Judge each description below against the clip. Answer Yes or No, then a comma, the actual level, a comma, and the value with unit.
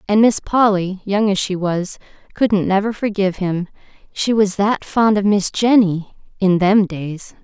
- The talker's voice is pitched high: Yes, high, 200 Hz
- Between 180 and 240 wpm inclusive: No, average, 145 wpm